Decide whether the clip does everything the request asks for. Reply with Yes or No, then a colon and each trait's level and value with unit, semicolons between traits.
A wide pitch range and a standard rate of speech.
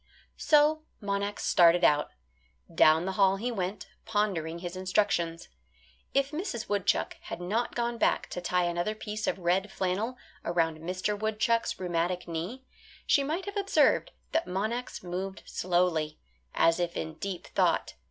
No: average, 4.3 semitones; average, 145 wpm